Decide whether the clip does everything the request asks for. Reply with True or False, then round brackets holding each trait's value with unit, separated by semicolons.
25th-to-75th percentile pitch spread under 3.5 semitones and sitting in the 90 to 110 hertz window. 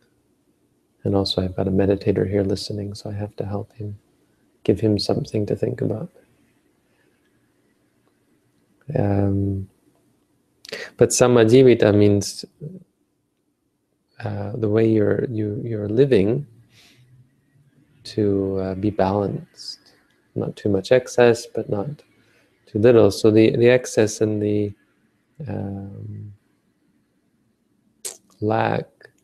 True (2.9 semitones; 105 Hz)